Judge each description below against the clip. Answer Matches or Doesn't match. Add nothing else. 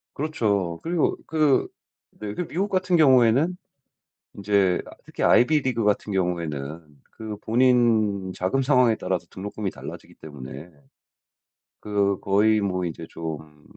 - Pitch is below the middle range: Matches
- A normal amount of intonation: Doesn't match